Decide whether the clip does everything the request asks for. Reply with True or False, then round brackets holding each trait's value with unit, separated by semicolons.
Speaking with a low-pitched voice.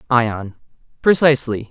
True (125 Hz)